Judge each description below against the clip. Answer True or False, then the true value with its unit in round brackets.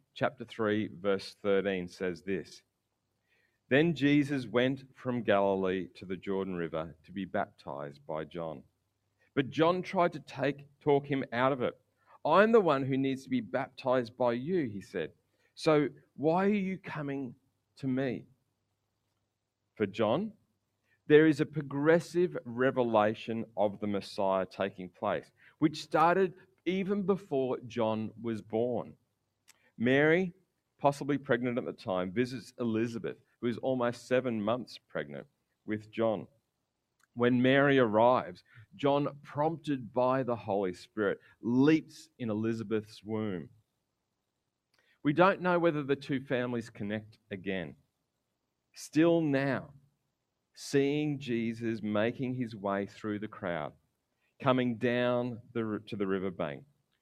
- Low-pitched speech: True (120 Hz)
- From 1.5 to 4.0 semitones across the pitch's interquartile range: False (5.1 semitones)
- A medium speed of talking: False (130 wpm)